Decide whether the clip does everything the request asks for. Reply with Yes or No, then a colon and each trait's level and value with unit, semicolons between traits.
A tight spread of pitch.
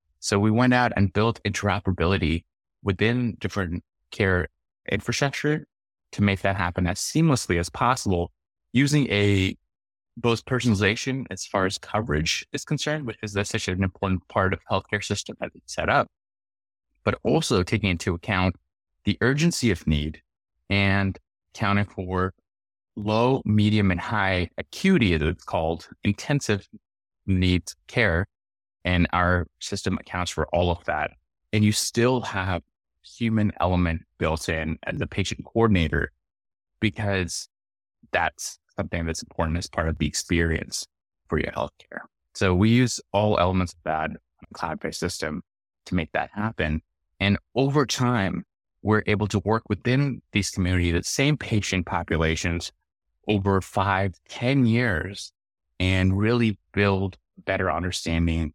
No: average, 3.8 semitones